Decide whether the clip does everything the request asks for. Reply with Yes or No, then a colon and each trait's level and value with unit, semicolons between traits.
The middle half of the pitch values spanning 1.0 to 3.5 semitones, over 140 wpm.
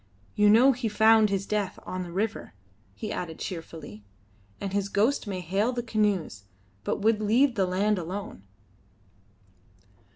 Yes: average, 3.0 semitones; average, 150 wpm